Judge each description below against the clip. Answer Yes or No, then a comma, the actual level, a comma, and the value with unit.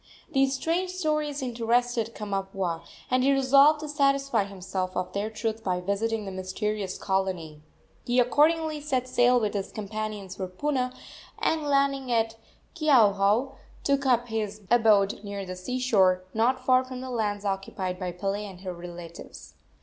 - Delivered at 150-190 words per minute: Yes, average, 155 wpm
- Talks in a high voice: Yes, high, 225 Hz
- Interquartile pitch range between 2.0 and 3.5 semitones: No, average, 5.3 semitones